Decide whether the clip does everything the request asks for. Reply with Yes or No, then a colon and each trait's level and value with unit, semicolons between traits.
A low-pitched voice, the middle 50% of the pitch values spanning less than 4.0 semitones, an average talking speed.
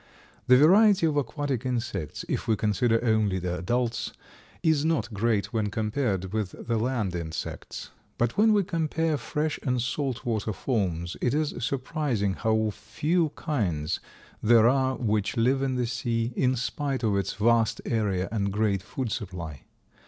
No: low, 115 Hz; average, 4.8 semitones; average, 155 wpm